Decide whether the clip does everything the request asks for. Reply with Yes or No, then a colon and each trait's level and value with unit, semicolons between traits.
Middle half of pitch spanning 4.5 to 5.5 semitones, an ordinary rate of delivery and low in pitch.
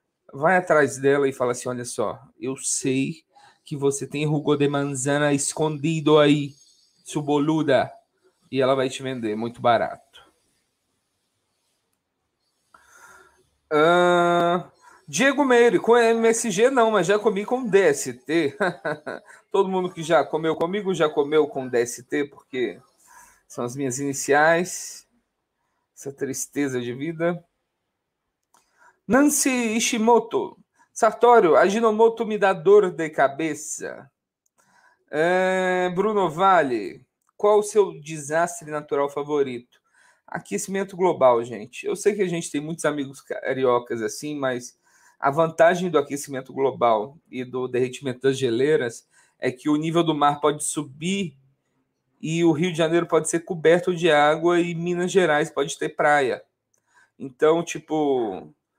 No: average, 5.2 semitones; average, 130 wpm; medium, 155 Hz